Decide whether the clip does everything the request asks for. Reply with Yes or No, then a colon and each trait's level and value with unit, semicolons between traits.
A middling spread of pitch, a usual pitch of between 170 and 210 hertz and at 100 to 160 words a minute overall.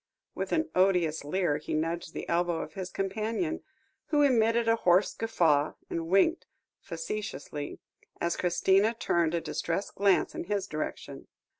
Yes: average, 4.4 semitones; medium, 185 Hz; average, 145 wpm